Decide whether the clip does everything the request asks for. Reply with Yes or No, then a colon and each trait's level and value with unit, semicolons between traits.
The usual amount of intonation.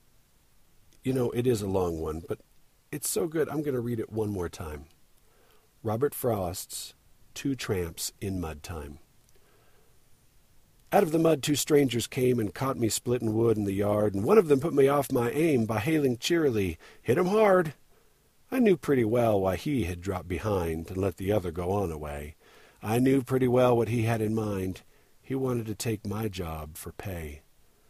No: wide, 5.9 semitones